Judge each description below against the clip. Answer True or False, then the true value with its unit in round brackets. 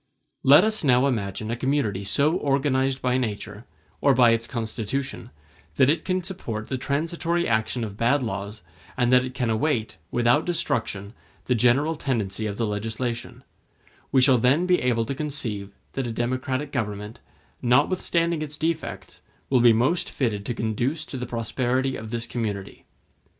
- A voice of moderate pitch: False (125 Hz)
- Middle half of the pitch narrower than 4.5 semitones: True (4.1 semitones)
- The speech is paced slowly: False (160 wpm)